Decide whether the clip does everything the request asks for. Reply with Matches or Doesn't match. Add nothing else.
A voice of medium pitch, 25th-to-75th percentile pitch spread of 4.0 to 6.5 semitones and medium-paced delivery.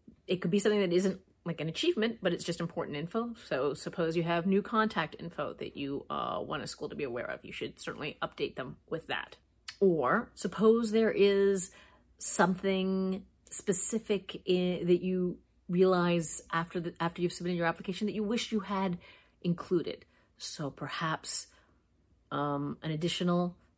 Doesn't match